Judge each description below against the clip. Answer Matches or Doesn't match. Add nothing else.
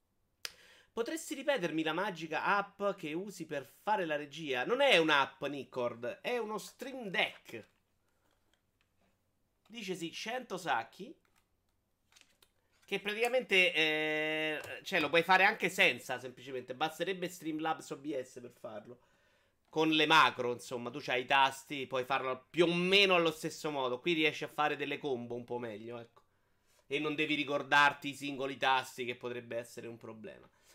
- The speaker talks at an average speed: Matches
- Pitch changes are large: Matches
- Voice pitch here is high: Doesn't match